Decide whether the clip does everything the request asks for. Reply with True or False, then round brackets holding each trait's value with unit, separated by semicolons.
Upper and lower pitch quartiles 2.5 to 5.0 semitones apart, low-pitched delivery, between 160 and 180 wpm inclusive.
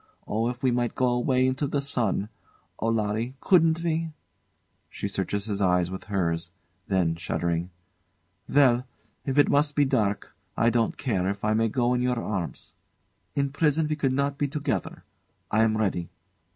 False (5.4 semitones; 120 Hz; 170 wpm)